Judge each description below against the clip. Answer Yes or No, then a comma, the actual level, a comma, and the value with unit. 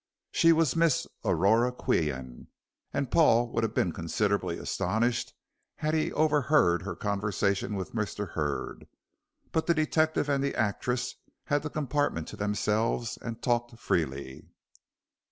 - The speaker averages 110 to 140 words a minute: Yes, slow, 135 wpm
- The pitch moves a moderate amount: No, wide, 6.5 semitones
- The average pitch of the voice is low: Yes, low, 115 Hz